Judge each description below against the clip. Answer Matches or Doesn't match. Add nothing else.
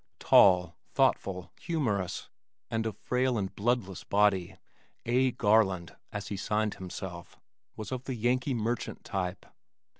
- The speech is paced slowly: Matches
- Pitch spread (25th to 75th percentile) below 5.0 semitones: Matches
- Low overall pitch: Matches